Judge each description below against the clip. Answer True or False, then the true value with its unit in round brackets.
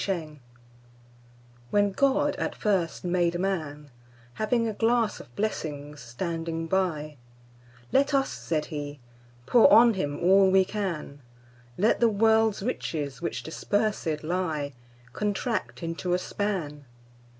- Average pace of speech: False (110 wpm)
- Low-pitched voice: False (170 Hz)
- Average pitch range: False (6.1 semitones)